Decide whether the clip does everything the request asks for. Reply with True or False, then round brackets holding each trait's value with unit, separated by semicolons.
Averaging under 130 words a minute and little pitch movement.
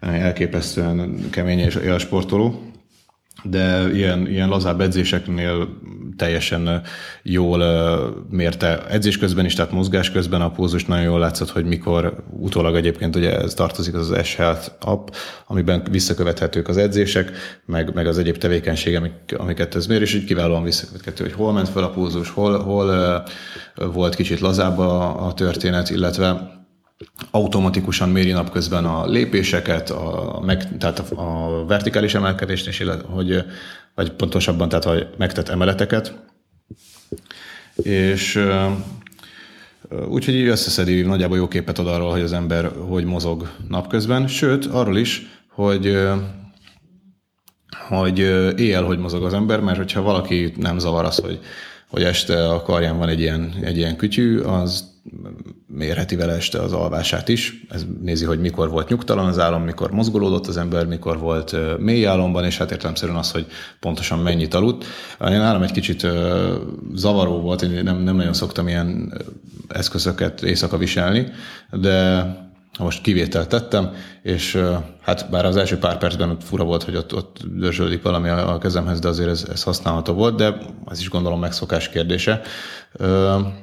False (150 wpm; 2.1 semitones)